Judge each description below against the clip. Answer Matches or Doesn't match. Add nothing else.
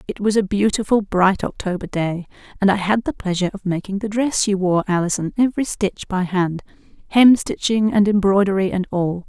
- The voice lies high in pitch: Matches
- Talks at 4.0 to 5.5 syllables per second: Matches